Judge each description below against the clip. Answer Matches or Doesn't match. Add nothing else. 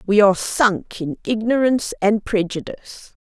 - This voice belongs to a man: Doesn't match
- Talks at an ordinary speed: Doesn't match